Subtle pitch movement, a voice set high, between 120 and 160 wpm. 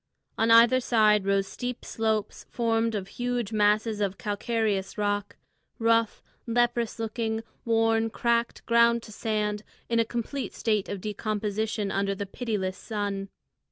Yes: narrow, 2.0 semitones; high, 220 Hz; slow, 135 wpm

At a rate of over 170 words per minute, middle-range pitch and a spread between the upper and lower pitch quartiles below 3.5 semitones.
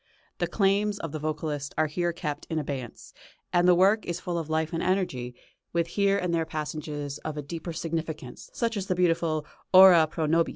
Yes: average, 200 wpm; medium, 165 Hz; average, 2.8 semitones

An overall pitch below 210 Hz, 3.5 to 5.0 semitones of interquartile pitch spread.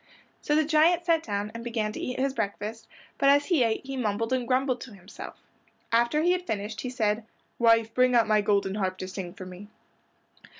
No: high, 230 Hz; average, 4.4 semitones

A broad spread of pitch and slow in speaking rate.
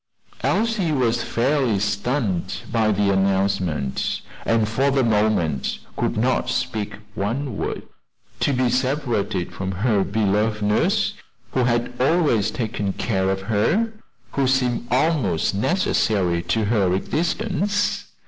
No: average, 4.9 semitones; slow, 120 wpm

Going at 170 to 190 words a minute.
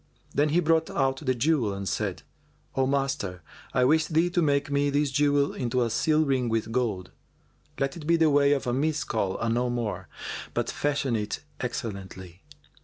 Yes: average, 180 wpm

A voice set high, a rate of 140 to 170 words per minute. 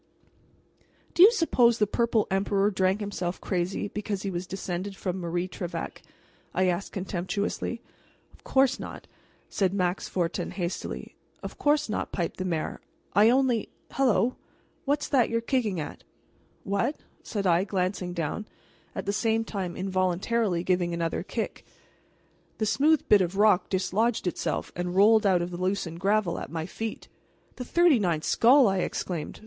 Yes: high, 195 Hz; average, 155 wpm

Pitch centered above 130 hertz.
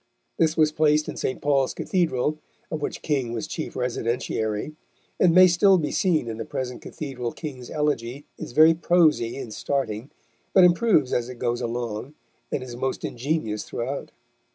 Yes: medium, 140 Hz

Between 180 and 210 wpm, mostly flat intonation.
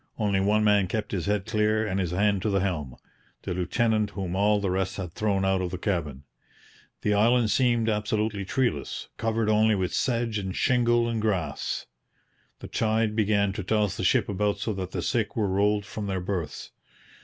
Yes: average, 190 wpm; narrow, 2.3 semitones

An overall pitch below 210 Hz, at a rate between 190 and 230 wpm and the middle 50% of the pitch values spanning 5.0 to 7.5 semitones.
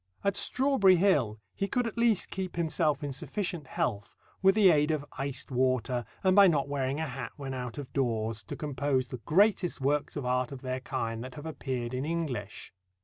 Yes: medium, 140 Hz; average, 200 wpm; wide, 5.4 semitones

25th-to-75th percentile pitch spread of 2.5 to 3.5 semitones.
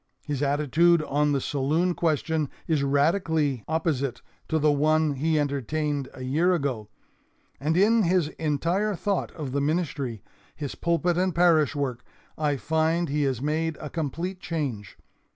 Yes: average, 2.9 semitones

